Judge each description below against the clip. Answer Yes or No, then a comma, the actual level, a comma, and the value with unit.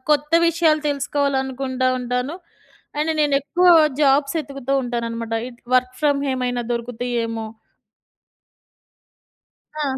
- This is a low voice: No, very high, 265 Hz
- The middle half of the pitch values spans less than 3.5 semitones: Yes, average, 2.8 semitones